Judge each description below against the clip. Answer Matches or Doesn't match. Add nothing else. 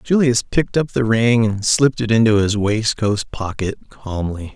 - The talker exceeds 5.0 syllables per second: Doesn't match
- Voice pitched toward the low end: Matches